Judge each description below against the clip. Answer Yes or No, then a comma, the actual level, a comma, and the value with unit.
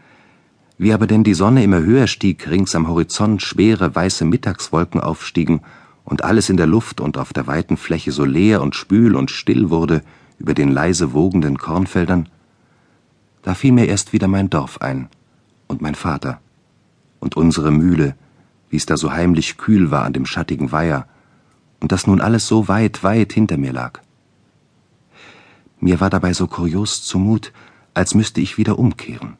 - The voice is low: Yes, very low, 95 Hz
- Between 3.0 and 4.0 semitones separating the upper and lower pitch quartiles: No, average, 4.5 semitones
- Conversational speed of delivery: Yes, average, 170 wpm